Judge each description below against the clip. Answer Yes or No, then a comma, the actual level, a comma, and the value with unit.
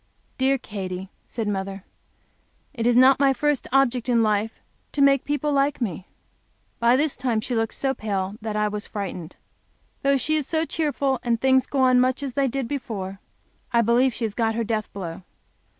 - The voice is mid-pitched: No, high, 240 Hz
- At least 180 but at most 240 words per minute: Yes, average, 190 wpm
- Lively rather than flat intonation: No, average, 4.3 semitones